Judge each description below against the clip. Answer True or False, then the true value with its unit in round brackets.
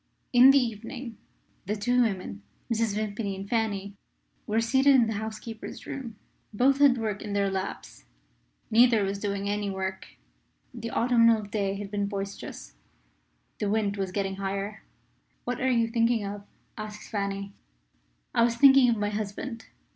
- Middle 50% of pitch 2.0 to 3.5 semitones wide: True (2.7 semitones)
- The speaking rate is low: False (155 wpm)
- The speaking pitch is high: True (215 Hz)